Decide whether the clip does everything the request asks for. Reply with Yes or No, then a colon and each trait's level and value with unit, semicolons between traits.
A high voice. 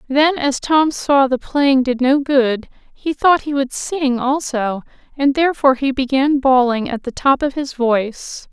Yes: very high, 270 Hz